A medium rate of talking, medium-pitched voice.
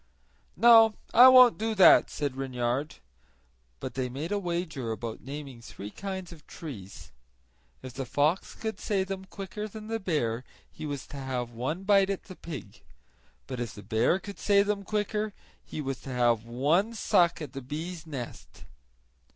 Yes: average, 170 wpm; medium, 155 Hz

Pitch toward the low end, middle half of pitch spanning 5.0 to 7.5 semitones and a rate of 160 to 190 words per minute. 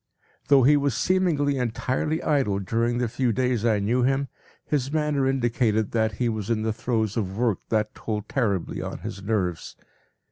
No: low, 120 Hz; average, 3.8 semitones; average, 175 wpm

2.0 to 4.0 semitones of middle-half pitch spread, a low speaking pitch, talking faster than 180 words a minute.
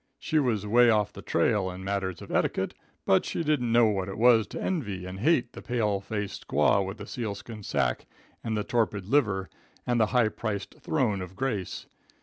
Yes: average, 3.5 semitones; low, 105 Hz; average, 195 wpm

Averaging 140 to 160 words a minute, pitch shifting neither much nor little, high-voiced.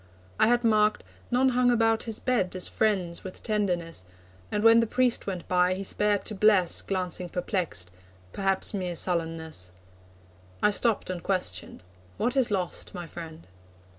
Yes: average, 155 wpm; average, 4.0 semitones; high, 195 Hz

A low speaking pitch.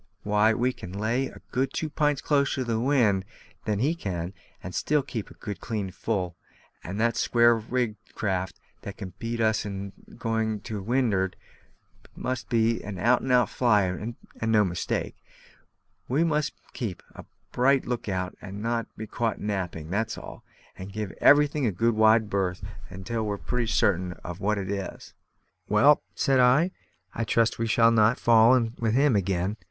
Yes: low, 110 Hz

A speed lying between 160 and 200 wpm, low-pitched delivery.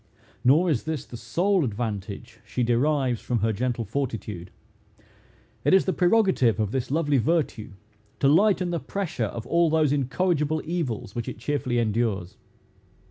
No: average, 150 wpm; low, 130 Hz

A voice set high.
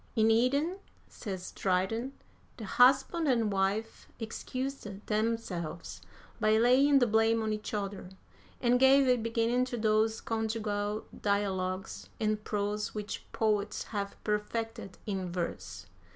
Yes: high, 220 Hz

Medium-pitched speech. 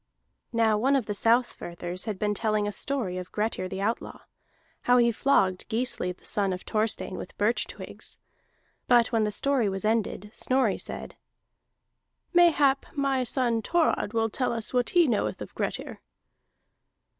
No: high, 225 Hz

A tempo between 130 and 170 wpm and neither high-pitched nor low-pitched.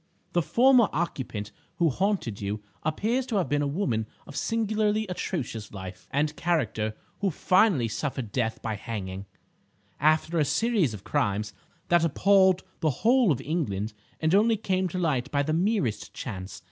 Yes: average, 160 wpm; medium, 155 Hz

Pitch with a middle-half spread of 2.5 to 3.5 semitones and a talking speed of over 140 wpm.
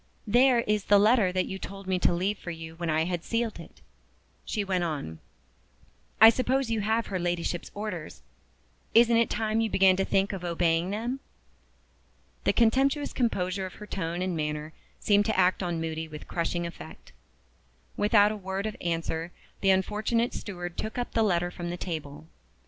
No: average, 4.1 semitones; average, 180 wpm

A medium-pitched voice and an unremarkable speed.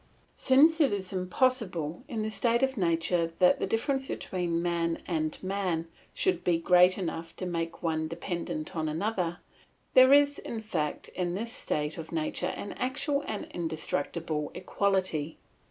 Yes: medium, 180 Hz; average, 155 wpm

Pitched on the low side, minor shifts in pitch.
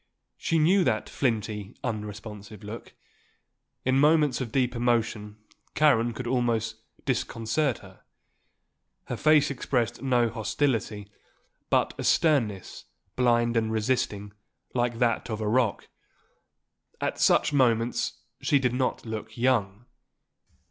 No: low, 120 Hz; average, 3.0 semitones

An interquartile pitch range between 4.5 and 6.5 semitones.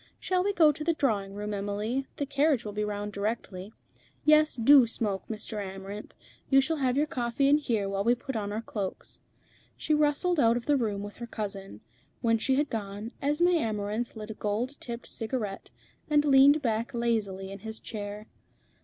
Yes: average, 5.2 semitones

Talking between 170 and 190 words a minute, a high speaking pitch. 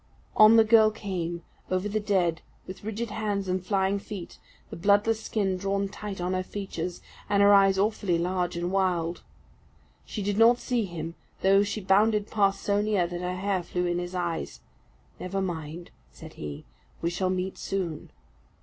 Yes: average, 175 wpm; high, 195 Hz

